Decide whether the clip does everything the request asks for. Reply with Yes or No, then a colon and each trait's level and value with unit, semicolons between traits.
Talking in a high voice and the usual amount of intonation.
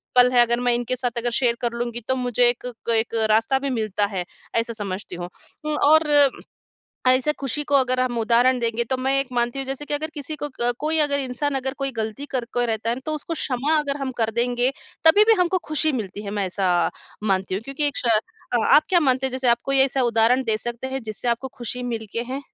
Yes: high, 245 Hz; average, 3.0 semitones